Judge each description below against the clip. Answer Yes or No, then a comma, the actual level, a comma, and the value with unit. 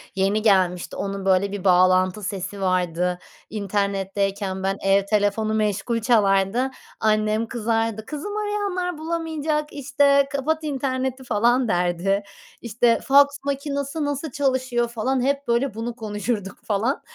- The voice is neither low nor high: No, high, 225 Hz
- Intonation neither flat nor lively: No, wide, 5.8 semitones